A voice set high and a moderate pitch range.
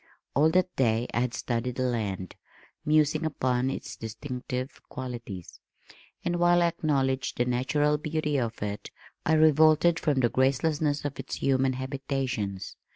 No: low, 135 Hz; average, 3.7 semitones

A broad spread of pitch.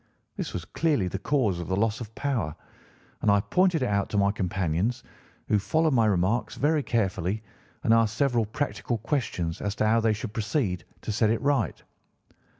No: average, 4.1 semitones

